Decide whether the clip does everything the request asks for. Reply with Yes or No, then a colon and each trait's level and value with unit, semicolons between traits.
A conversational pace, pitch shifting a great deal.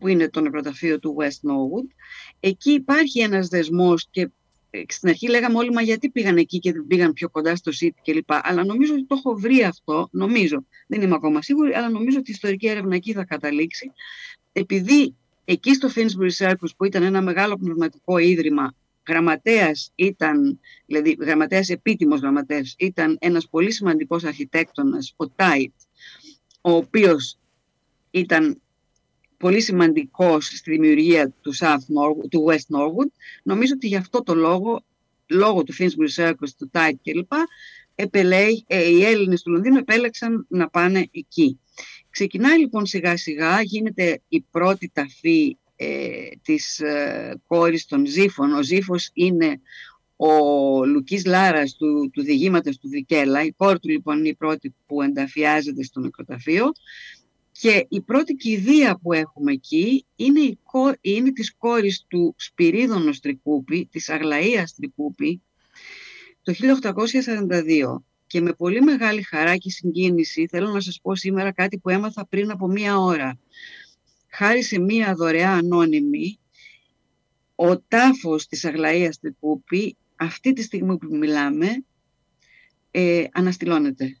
Yes: average, 145 wpm; wide, 6.6 semitones